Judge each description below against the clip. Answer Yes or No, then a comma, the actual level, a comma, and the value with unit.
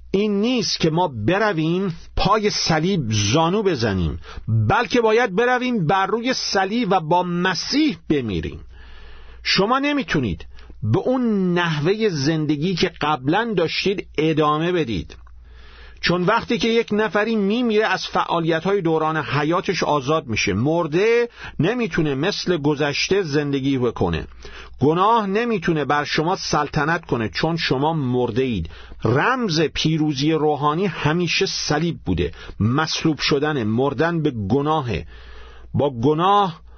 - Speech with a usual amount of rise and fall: No, wide, 6.7 semitones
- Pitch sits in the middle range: Yes, medium, 160 Hz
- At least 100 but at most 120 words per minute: Yes, average, 115 wpm